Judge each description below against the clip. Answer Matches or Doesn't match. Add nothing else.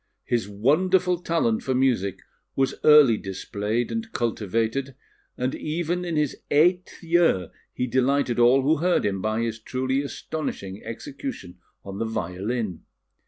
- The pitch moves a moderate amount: Doesn't match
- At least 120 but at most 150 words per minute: Matches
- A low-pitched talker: Matches